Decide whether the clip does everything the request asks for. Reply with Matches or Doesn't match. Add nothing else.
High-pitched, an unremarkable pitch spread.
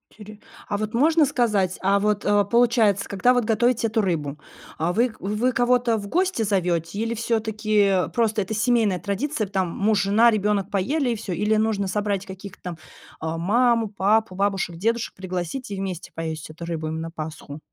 Matches